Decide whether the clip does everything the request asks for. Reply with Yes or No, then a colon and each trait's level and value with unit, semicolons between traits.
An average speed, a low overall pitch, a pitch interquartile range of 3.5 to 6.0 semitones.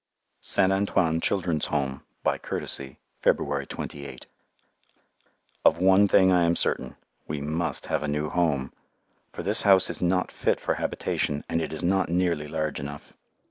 Yes: average, 155 wpm; very low, 85 Hz; average, 3.9 semitones